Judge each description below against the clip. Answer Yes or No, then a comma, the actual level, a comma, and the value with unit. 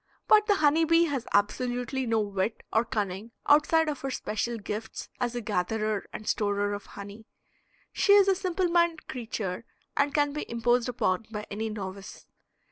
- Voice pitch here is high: Yes, high, 235 Hz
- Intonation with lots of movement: Yes, wide, 5.9 semitones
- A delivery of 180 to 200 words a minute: No, average, 170 wpm